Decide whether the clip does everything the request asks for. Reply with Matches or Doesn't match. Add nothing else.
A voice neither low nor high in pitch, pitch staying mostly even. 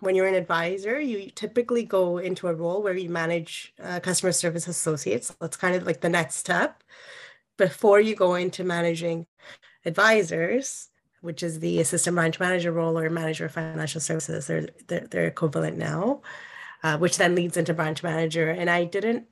Matches